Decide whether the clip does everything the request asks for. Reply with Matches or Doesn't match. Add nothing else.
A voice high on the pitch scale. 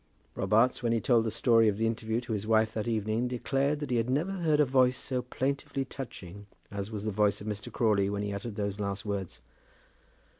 Doesn't match